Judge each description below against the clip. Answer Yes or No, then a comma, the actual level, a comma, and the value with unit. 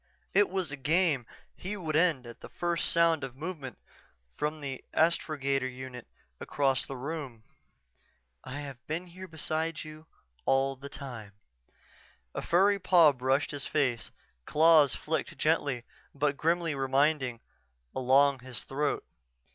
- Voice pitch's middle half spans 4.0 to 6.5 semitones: No, average, 3.5 semitones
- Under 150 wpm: Yes, slow, 135 wpm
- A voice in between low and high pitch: Yes, medium, 145 Hz